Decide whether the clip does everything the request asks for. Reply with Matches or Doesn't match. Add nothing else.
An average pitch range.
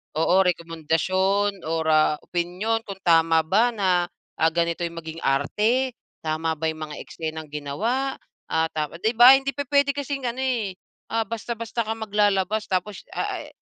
Doesn't match